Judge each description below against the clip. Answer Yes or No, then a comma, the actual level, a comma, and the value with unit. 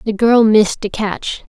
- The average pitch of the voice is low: No, high, 215 Hz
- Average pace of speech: Yes, average, 190 wpm